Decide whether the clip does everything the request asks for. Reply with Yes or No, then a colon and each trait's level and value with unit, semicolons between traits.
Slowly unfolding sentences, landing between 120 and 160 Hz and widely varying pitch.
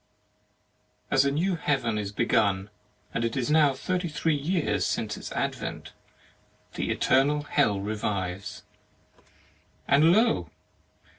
Yes: slow, 120 wpm; medium, 140 Hz; wide, 6.7 semitones